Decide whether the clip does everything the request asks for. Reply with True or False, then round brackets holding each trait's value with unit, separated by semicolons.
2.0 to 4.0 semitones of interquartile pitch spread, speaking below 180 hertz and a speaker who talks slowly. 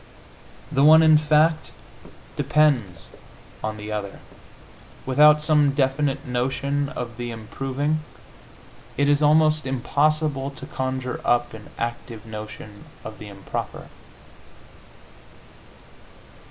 False (4.4 semitones; 135 Hz; 100 wpm)